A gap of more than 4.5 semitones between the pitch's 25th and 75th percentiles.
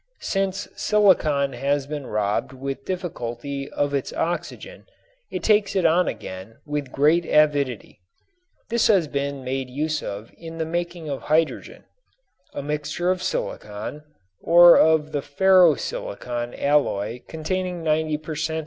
No: average, 3.9 semitones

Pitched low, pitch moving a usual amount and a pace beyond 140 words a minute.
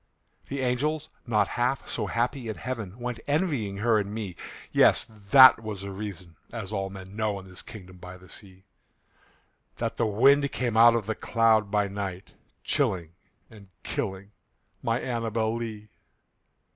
Yes: low, 110 Hz; average, 3.3 semitones; average, 160 wpm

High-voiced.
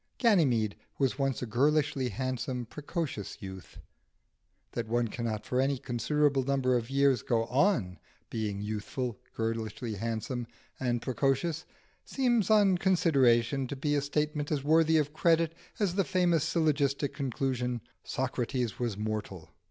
No: low, 135 Hz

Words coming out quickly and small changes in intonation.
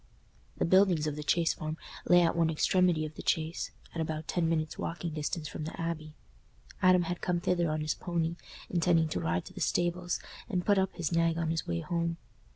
Yes: fast, 210 wpm; narrow, 2.0 semitones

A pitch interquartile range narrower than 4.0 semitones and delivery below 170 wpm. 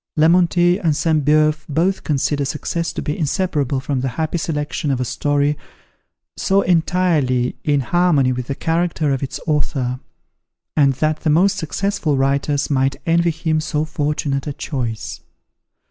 Yes: average, 3.2 semitones; average, 150 wpm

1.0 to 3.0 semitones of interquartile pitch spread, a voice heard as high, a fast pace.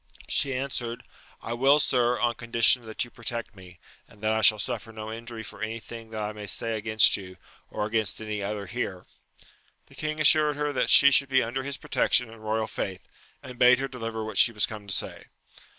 No: narrow, 2.6 semitones; low, 115 Hz; fast, 215 wpm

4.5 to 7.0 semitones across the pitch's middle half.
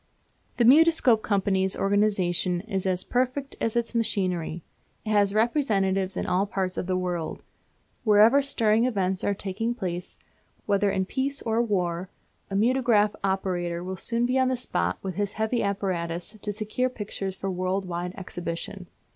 No: average, 3.7 semitones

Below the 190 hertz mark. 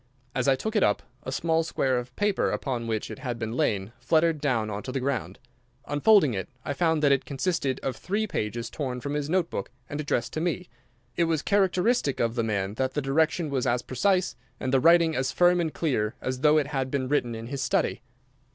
Yes: medium, 140 Hz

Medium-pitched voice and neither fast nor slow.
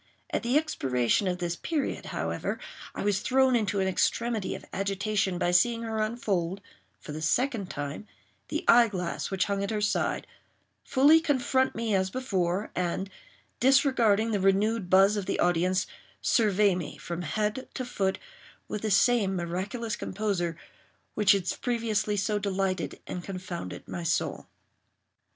No: high, 200 Hz; average, 150 wpm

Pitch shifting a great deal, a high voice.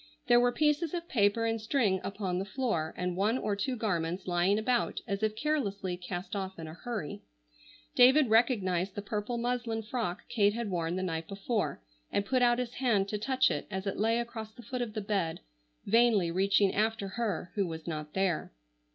No: average, 4.1 semitones; high, 210 Hz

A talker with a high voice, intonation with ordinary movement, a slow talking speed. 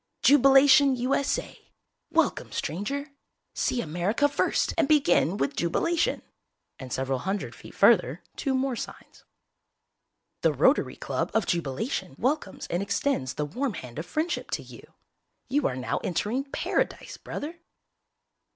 No: high, 245 Hz; wide, 8.7 semitones; slow, 130 wpm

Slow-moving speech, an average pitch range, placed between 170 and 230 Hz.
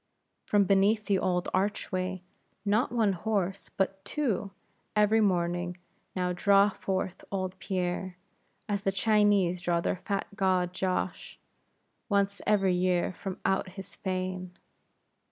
No: slow, 125 wpm; narrow, 1.8 semitones; high, 190 Hz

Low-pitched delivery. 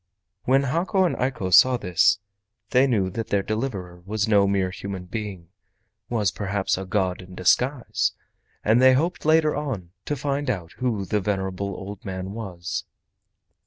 Yes: low, 100 Hz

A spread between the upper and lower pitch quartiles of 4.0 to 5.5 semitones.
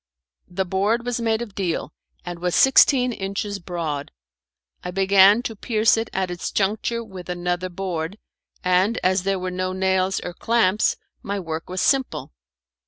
No: average, 3.2 semitones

